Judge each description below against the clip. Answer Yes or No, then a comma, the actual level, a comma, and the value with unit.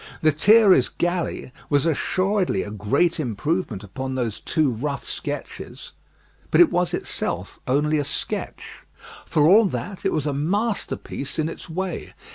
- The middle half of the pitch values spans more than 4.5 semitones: Yes, average, 5.0 semitones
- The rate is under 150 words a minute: Yes, average, 140 wpm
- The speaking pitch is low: No, medium, 155 Hz